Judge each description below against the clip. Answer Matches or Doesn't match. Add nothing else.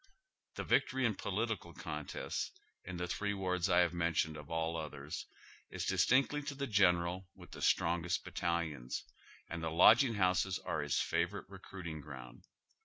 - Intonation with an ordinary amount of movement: Matches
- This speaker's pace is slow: Doesn't match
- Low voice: Matches